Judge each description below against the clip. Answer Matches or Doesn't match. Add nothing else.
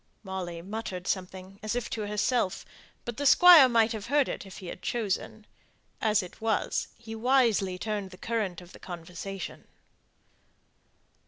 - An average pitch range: Matches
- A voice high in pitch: Matches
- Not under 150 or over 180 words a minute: Matches